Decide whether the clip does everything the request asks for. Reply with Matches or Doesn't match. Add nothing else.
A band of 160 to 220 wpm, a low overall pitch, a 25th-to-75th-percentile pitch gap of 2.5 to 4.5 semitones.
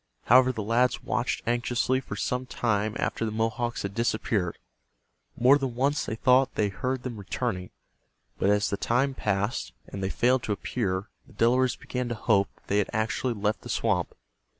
Matches